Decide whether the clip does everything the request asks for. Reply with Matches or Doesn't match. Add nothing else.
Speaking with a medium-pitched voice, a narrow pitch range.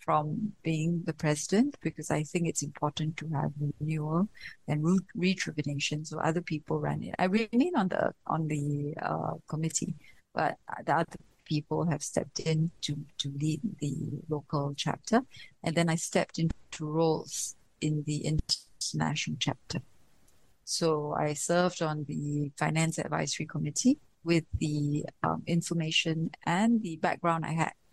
Matches